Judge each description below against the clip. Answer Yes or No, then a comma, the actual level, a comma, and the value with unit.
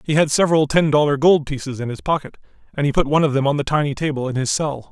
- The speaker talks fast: Yes, fast, 280 wpm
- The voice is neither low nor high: Yes, medium, 145 Hz